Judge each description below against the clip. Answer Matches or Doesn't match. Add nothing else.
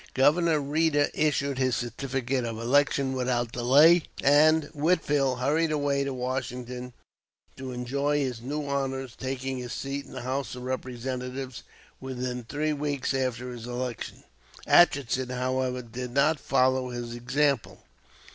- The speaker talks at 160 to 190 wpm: Doesn't match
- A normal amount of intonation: Doesn't match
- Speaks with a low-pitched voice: Matches